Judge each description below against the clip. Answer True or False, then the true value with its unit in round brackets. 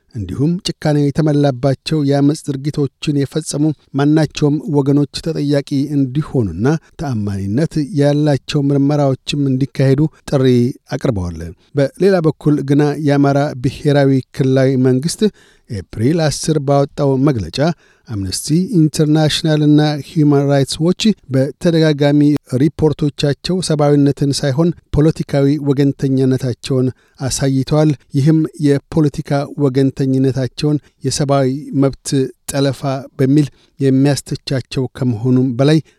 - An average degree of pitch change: False (2.2 semitones)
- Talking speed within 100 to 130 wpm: False (85 wpm)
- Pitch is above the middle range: False (140 Hz)